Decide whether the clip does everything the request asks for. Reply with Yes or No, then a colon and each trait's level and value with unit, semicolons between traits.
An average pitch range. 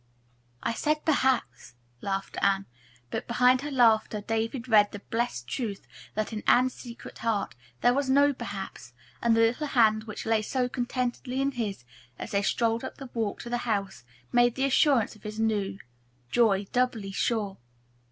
Yes: average, 3.4 semitones